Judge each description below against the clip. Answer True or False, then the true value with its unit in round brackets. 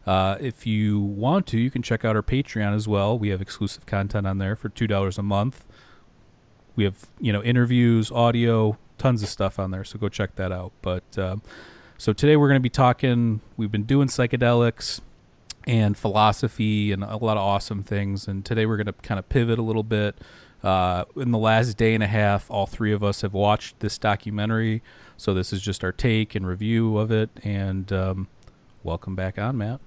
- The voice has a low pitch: True (105 Hz)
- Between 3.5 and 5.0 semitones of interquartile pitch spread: False (2.8 semitones)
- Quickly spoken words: True (210 wpm)